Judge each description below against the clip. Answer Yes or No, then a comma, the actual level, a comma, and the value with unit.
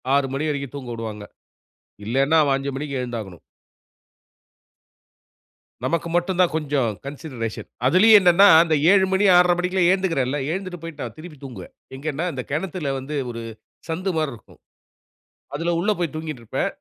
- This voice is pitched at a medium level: Yes, medium, 150 Hz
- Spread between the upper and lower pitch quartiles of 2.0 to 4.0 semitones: No, average, 4.8 semitones